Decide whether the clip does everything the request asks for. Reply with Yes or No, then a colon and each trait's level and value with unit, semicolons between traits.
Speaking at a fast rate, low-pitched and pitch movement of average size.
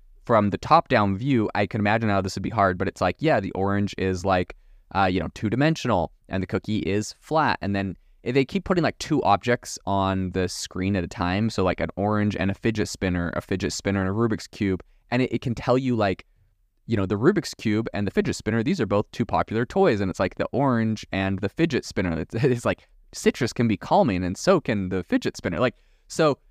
Yes: fast, 240 wpm; low, 100 Hz; average, 3.3 semitones